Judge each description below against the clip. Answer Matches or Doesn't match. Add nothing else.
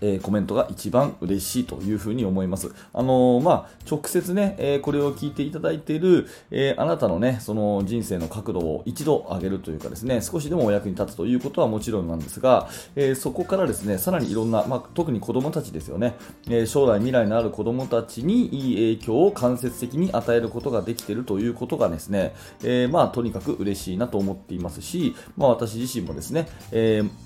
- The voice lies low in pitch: Matches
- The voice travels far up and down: Doesn't match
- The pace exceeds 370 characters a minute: Matches